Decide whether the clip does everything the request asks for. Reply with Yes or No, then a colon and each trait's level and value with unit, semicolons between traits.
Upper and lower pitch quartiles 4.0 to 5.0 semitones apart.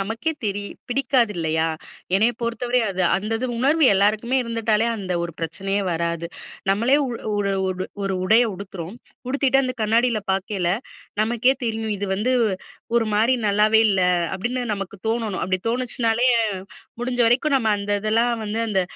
No: average, 3.5 semitones